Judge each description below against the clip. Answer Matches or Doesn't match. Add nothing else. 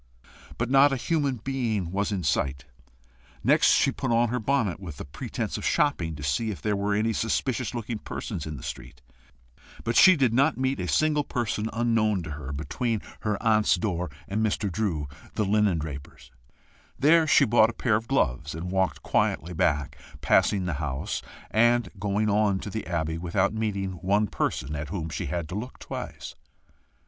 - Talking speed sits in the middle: Matches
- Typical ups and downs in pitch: Doesn't match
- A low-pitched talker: Matches